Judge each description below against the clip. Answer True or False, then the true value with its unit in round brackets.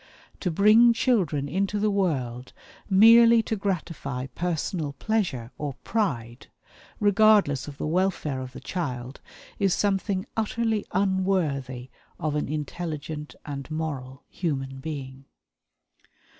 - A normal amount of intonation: False (6.4 semitones)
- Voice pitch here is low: False (160 Hz)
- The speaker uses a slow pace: True (115 wpm)